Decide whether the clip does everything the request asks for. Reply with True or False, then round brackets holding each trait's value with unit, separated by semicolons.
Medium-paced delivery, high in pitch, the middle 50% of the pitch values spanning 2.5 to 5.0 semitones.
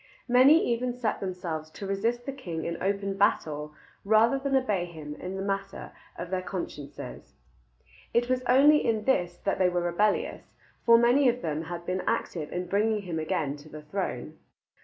False (180 wpm; 195 Hz; 5.6 semitones)